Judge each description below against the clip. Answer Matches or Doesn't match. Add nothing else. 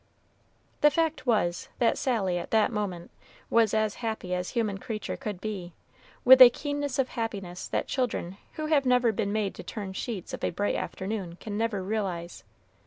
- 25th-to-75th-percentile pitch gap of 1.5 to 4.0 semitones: Doesn't match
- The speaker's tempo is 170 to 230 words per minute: Matches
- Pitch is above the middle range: Matches